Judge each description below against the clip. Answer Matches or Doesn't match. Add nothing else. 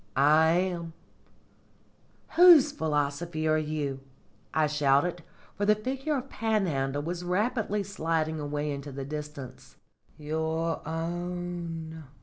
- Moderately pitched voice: Matches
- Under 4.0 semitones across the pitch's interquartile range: Matches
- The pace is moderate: Doesn't match